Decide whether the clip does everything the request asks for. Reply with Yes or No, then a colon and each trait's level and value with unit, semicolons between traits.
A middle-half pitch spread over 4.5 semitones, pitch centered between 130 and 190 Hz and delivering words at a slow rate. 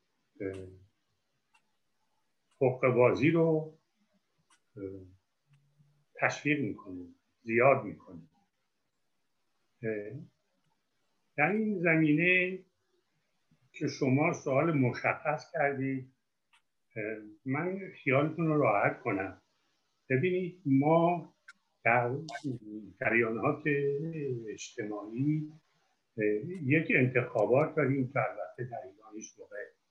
Yes: average, 5.2 semitones; medium, 140 Hz; slow, 65 wpm